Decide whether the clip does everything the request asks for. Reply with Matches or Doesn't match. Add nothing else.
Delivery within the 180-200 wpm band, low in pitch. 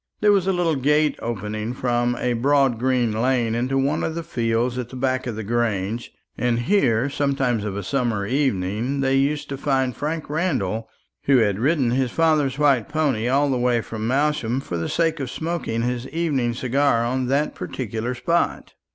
Matches